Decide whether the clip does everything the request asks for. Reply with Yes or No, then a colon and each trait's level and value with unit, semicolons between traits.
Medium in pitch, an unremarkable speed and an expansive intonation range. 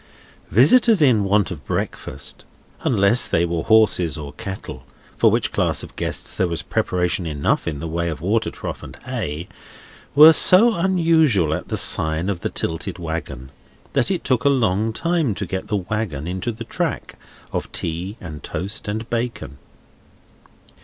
No: very low, 95 Hz; average, 160 wpm; wide, 6.2 semitones